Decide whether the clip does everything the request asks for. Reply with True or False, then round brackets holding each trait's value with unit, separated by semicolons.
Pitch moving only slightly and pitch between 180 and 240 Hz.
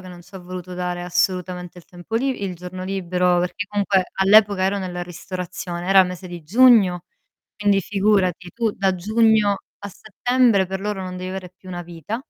True (2.2 semitones; 185 Hz)